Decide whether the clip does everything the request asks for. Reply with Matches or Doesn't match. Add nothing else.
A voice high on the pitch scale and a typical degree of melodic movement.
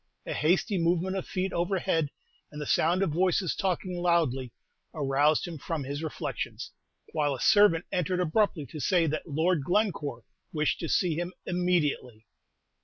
Doesn't match